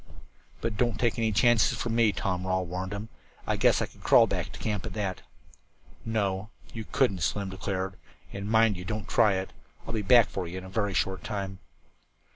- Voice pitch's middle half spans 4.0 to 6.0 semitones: No, average, 2.9 semitones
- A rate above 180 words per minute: Yes, fast, 205 wpm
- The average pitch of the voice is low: Yes, low, 100 Hz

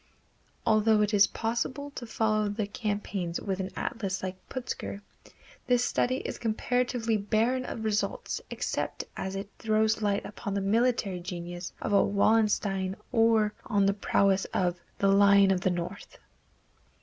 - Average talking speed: Yes, average, 150 wpm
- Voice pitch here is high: Yes, high, 205 Hz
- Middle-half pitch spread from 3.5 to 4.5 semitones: No, narrow, 2.4 semitones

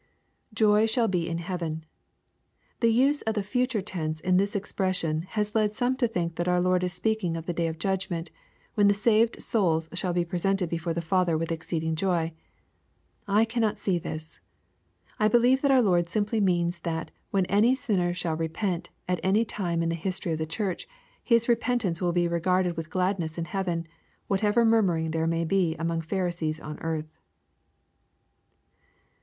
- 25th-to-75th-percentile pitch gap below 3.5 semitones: No, average, 4.1 semitones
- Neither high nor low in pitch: Yes, medium, 180 Hz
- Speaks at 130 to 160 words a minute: No, average, 180 wpm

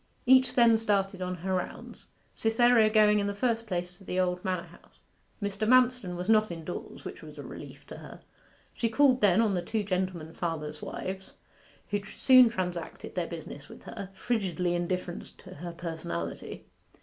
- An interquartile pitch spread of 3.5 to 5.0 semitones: Yes, average, 4.1 semitones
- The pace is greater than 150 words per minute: Yes, average, 175 wpm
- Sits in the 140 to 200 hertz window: Yes, high, 190 Hz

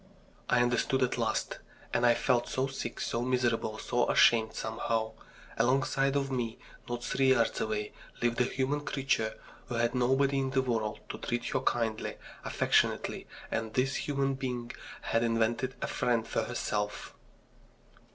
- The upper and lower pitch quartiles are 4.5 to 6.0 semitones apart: No, narrow, 2.5 semitones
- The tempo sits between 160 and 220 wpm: No, average, 150 wpm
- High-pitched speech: No, low, 120 Hz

